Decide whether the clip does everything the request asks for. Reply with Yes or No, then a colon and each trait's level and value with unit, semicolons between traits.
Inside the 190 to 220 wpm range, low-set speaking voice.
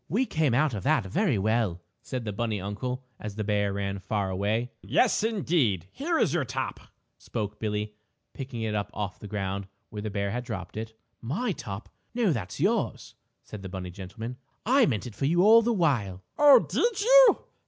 Yes: average, 195 wpm; low, 110 Hz